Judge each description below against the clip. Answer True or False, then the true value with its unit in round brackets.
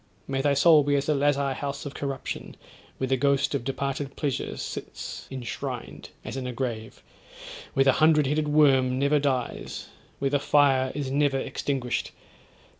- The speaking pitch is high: False (140 Hz)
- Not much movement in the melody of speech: True (1.5 semitones)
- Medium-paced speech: True (165 wpm)